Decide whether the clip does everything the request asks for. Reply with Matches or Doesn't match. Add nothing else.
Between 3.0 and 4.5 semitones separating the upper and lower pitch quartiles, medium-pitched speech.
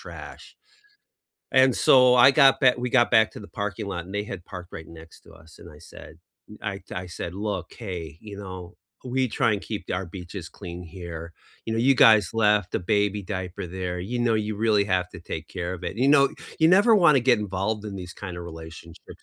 Doesn't match